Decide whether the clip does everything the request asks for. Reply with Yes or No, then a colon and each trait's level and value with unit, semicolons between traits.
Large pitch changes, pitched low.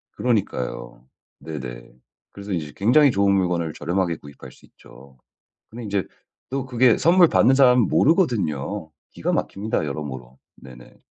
Yes: wide, 8.9 semitones; very low, 95 Hz